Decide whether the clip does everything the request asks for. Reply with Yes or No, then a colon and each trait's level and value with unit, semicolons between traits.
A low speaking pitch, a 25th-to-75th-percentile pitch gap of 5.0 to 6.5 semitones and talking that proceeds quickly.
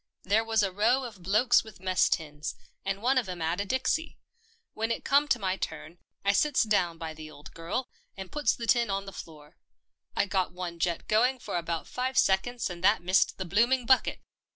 No: high, 195 Hz; wide, 5.4 semitones; fast, 210 wpm